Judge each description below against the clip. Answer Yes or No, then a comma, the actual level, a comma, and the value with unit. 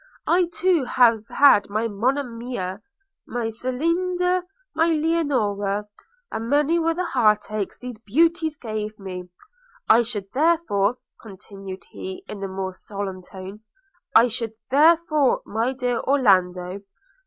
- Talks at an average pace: No, slow, 125 wpm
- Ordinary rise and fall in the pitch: No, wide, 6.9 semitones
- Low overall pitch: No, high, 230 Hz